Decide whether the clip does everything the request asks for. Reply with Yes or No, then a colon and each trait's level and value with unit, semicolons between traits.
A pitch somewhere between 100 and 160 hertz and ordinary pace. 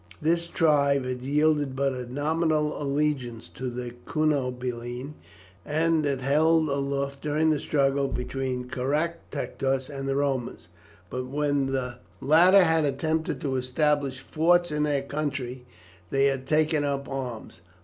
No: medium, 140 Hz; slow, 130 wpm